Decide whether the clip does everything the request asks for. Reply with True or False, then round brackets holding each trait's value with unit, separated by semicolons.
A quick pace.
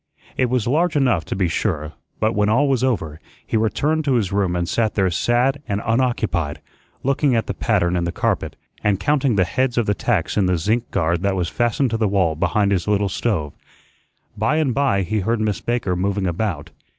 True (210 wpm)